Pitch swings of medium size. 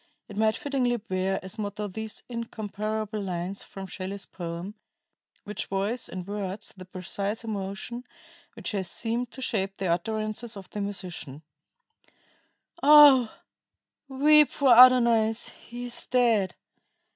Yes: average, 3.6 semitones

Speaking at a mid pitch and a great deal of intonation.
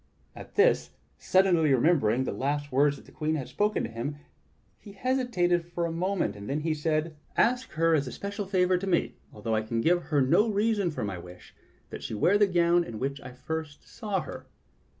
Yes: medium, 165 Hz; wide, 5.9 semitones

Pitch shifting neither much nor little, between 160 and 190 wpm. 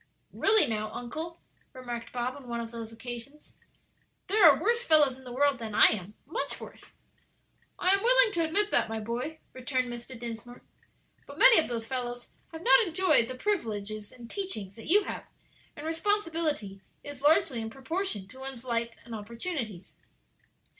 No: wide, 6.0 semitones; average, 170 wpm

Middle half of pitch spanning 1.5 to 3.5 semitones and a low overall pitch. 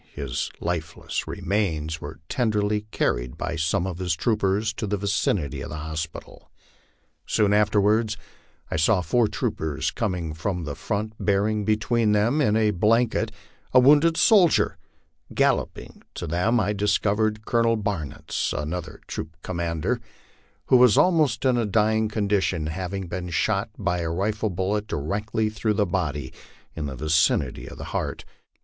No: average, 4.6 semitones; low, 100 Hz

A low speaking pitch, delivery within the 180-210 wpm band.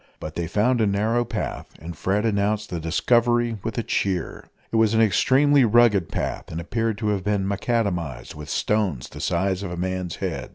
Yes: low, 105 Hz; average, 195 wpm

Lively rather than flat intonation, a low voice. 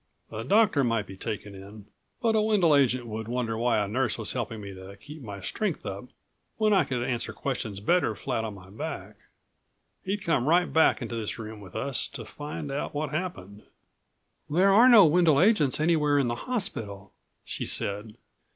Yes: wide, 7.3 semitones; low, 125 Hz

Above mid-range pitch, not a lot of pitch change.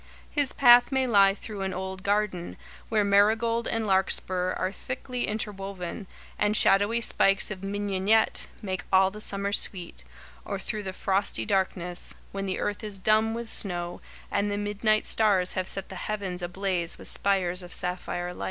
Yes: high, 200 Hz; narrow, 2.2 semitones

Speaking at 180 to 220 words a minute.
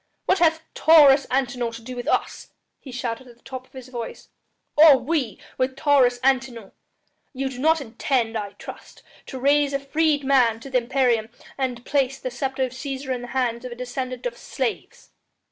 Yes: average, 185 wpm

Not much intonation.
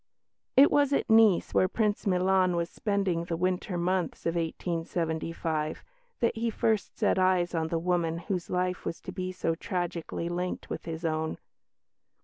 Yes: narrow, 2.2 semitones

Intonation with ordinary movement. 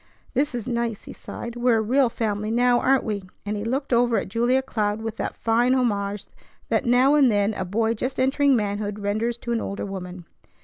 Yes: average, 3.2 semitones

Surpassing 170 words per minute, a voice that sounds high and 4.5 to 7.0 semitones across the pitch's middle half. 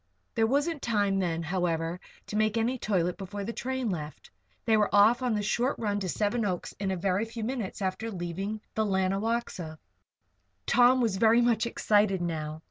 No: average, 180 wpm; high, 205 Hz; average, 3.7 semitones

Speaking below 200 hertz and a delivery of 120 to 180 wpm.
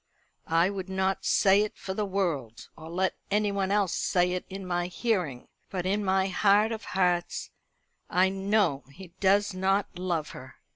Yes: high, 190 Hz; average, 165 wpm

